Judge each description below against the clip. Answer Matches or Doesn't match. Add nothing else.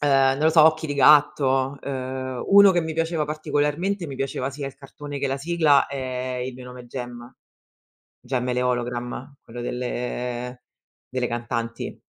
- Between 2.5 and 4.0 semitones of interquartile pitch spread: Matches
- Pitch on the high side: Doesn't match